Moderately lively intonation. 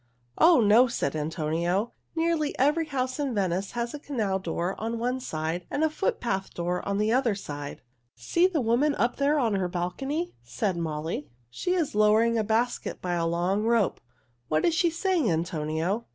No: wide, 7.7 semitones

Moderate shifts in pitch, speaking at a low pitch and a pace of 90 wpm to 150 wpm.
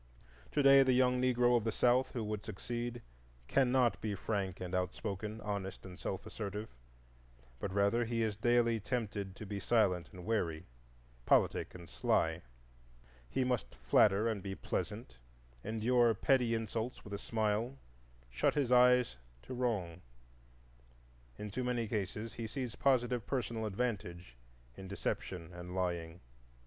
Yes: average, 4.0 semitones; low, 110 Hz; average, 145 wpm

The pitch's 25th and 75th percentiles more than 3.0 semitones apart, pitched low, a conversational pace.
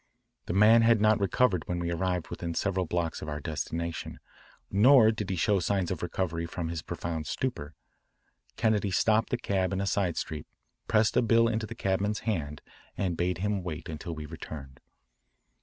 Yes: average, 4.2 semitones; very low, 95 Hz; average, 180 wpm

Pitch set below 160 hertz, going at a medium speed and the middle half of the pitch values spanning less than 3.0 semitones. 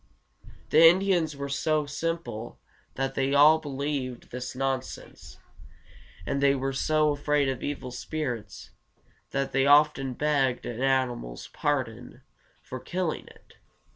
No: medium, 140 Hz; slow, 125 wpm; narrow, 2.6 semitones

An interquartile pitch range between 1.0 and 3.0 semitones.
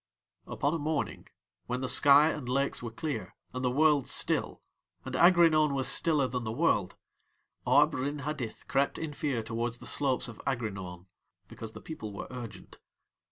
No: average, 4.2 semitones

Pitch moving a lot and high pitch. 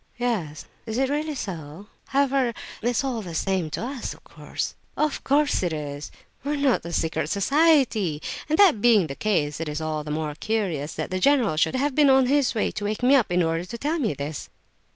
Yes: wide, 8.9 semitones; high, 215 Hz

